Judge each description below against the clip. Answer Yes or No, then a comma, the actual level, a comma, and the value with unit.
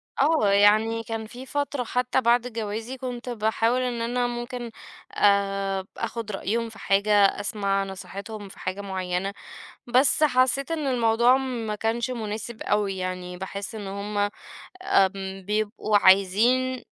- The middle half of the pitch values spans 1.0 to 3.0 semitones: No, average, 3.7 semitones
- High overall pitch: Yes, high, 220 Hz